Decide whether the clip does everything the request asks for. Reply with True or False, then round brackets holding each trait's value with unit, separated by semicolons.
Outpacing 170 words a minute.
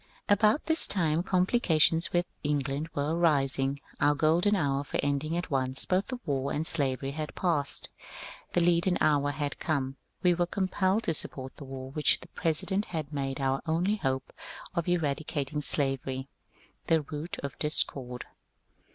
False (155 wpm)